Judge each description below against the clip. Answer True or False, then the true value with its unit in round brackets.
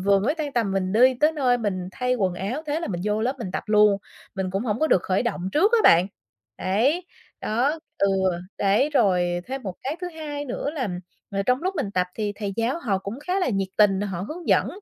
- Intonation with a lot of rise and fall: True (6.7 semitones)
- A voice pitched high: True (220 Hz)